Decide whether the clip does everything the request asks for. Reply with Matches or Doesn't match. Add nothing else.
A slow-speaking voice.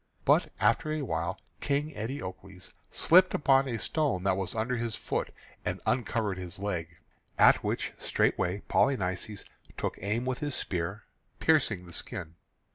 Doesn't match